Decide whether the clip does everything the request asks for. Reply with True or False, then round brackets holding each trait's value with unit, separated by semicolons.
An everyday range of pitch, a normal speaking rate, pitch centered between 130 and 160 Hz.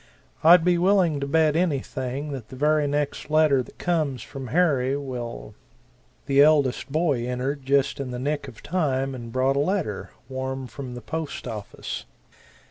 True (3.1 semitones; 170 wpm; 140 Hz)